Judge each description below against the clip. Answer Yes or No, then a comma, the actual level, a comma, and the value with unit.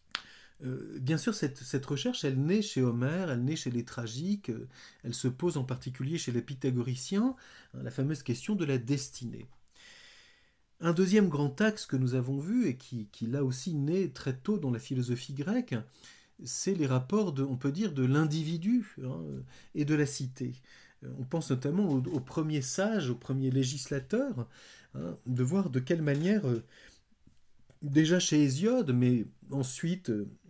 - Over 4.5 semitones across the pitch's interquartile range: Yes, average, 4.9 semitones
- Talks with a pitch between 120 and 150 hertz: Yes, medium, 140 Hz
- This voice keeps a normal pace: Yes, average, 170 wpm